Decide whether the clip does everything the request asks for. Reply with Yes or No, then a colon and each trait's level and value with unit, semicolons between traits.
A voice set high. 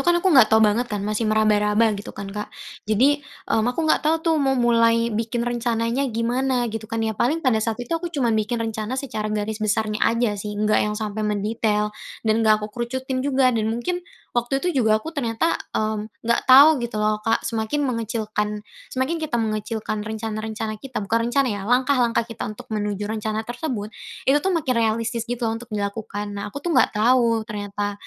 Yes: high, 225 Hz